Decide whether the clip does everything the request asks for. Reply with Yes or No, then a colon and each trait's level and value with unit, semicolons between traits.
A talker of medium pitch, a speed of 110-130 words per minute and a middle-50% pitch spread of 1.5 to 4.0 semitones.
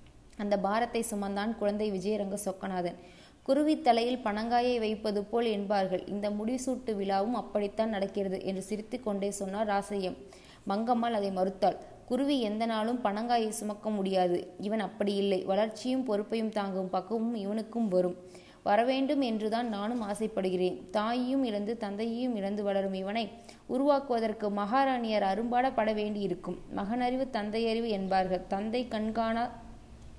No: high, 215 Hz; average, 115 wpm; average, 2.7 semitones